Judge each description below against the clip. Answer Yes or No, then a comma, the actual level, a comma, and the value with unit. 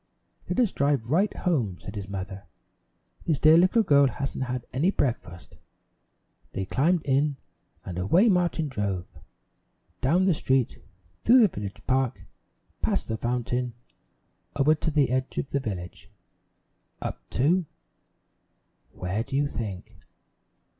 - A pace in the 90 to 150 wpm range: Yes, slow, 135 wpm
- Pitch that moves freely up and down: Yes, wide, 6.3 semitones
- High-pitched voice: No, low, 135 Hz